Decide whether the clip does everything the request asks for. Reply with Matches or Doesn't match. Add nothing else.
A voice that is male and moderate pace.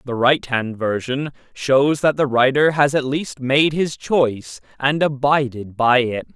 Matches